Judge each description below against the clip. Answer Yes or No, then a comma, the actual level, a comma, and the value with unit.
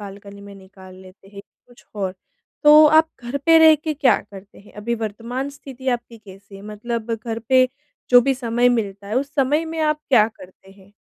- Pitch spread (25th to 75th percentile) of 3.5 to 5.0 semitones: Yes, average, 4.7 semitones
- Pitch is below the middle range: No, high, 230 Hz